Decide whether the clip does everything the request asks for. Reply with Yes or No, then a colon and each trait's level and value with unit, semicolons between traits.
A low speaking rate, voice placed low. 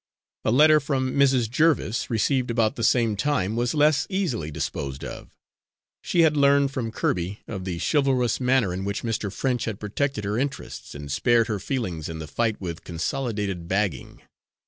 No: average, 170 wpm; low, 115 Hz